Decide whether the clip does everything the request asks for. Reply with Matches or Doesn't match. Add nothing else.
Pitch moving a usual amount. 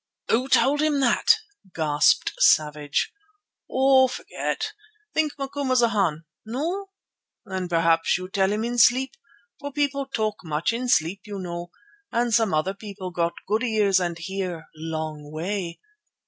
Doesn't match